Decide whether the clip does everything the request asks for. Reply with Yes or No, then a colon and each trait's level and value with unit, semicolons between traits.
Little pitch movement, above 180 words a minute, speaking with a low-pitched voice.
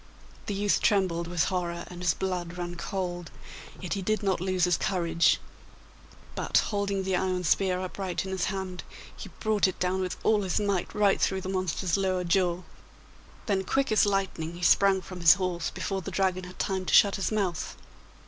No: narrow, 1.6 semitones; average, 190 wpm; medium, 185 Hz